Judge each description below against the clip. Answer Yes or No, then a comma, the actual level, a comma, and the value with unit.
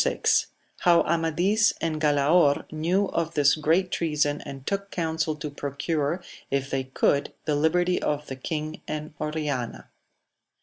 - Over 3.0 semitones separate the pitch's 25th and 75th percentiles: No, narrow, 2.6 semitones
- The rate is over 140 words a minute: No, slow, 135 wpm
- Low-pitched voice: No, medium, 155 Hz